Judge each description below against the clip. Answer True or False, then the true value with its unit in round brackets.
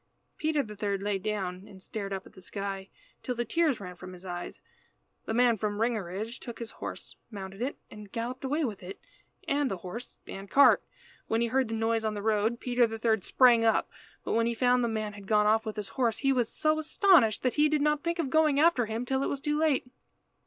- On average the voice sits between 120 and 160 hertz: False (225 Hz)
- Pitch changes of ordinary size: True (4.3 semitones)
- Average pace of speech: False (235 wpm)